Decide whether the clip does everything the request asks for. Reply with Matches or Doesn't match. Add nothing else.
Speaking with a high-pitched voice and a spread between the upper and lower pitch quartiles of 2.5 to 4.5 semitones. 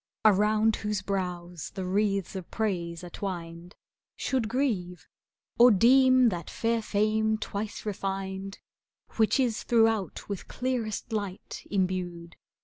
Matches